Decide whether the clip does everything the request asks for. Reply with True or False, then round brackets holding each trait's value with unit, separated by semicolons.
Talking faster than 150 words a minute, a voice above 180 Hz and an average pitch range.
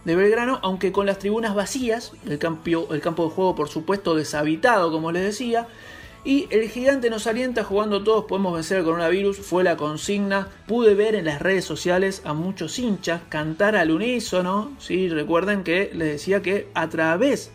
True (190 wpm; 190 Hz; 4.4 semitones)